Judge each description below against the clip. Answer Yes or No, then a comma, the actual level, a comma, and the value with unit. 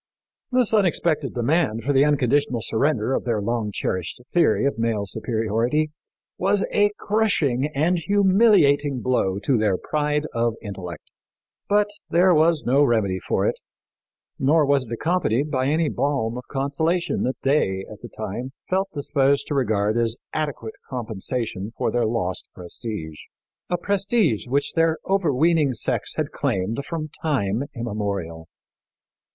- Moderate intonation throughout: No, wide, 6.0 semitones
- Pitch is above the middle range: No, low, 135 Hz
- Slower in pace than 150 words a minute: Yes, average, 140 wpm